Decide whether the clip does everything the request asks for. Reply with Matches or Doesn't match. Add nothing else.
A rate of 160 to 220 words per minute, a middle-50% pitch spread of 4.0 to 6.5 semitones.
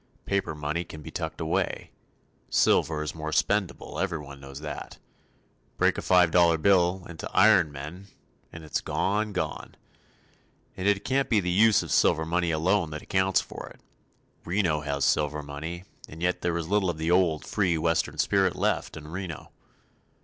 Doesn't match